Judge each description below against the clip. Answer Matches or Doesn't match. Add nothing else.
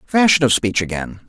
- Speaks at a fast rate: Doesn't match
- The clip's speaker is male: Matches